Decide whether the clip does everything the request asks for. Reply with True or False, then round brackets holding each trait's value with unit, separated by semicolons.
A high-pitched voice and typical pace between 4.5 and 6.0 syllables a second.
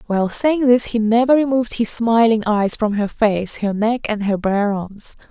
True (220 Hz; 4.7 syllables/s)